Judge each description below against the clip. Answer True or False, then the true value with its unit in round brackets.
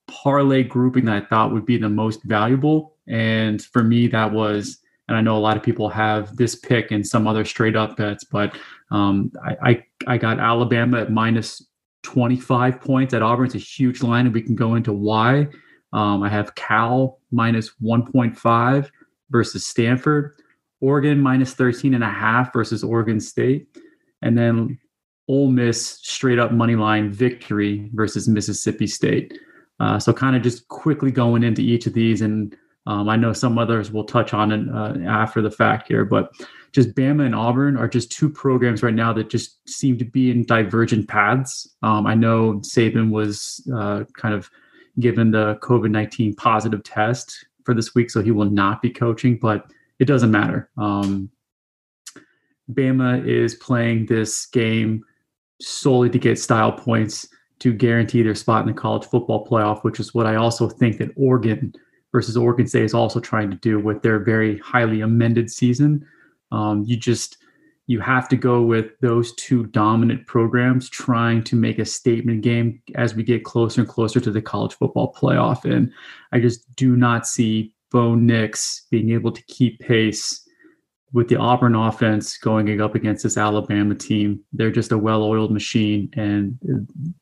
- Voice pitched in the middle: False (115 Hz)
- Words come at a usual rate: True (175 wpm)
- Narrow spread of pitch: True (2.3 semitones)